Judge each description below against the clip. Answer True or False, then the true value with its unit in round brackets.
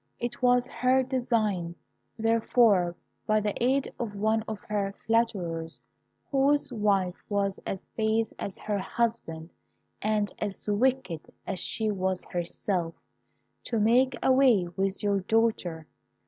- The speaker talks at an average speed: False (125 wpm)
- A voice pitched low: False (215 Hz)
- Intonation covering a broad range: False (3.7 semitones)